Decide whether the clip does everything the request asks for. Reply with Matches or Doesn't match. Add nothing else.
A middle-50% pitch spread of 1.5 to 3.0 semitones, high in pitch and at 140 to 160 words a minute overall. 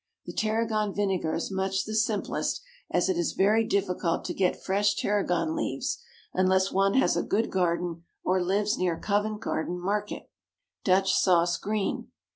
Matches